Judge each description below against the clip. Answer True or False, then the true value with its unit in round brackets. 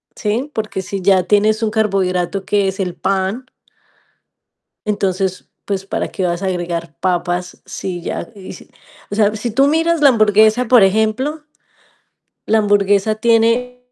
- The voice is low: False (205 Hz)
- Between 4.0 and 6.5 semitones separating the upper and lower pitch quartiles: False (2.9 semitones)